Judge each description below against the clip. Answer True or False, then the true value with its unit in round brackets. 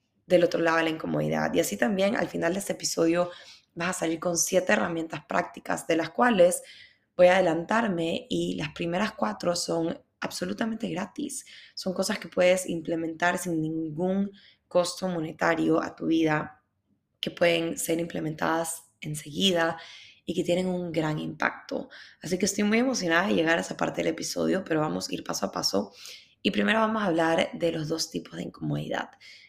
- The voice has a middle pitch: True (170 Hz)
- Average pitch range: False (2.2 semitones)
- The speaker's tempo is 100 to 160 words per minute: False (175 wpm)